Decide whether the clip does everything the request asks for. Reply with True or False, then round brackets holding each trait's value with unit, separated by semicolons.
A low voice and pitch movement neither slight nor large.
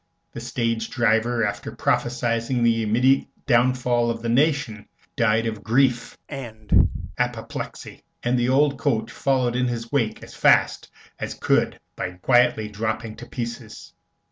False (120 Hz; 2.0 semitones)